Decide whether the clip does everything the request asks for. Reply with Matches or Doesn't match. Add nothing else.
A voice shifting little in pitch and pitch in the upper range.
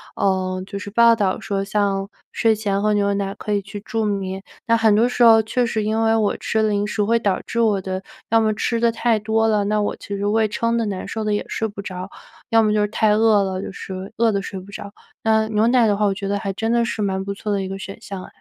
Matches